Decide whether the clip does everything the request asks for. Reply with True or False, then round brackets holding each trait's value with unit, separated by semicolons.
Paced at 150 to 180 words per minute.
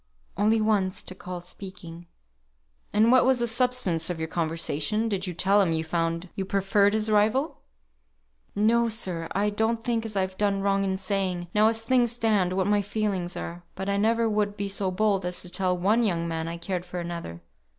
False (200 wpm)